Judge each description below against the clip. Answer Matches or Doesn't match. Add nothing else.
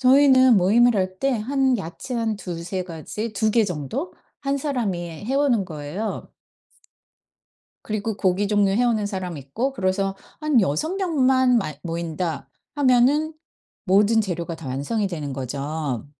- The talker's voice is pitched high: Matches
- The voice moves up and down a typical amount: Doesn't match